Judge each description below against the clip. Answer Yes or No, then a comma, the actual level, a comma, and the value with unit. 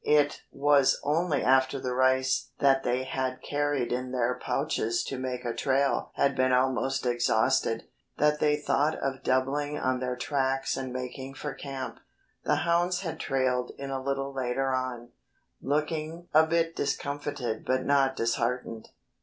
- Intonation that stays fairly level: Yes, narrow, 2.2 semitones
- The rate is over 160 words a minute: No, average, 155 wpm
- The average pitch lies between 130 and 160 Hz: Yes, low, 135 Hz